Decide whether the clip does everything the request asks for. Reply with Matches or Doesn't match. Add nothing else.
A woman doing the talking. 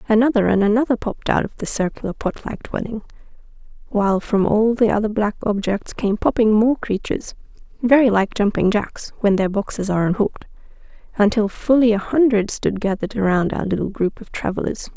Matches